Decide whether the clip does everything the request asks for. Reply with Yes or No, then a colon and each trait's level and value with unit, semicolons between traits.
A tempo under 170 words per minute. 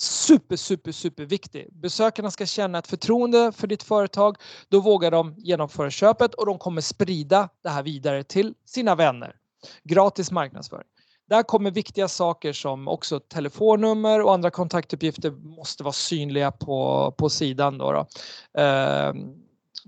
Yes: average, 145 wpm